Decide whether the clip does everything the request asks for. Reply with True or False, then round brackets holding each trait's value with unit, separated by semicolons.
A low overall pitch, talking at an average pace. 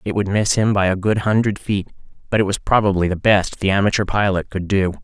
False (100 Hz; 240 wpm)